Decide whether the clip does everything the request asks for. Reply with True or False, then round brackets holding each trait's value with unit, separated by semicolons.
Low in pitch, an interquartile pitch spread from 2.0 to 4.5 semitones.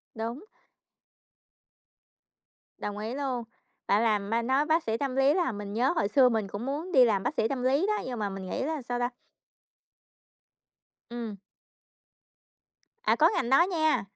False (245 Hz; 4.2 semitones)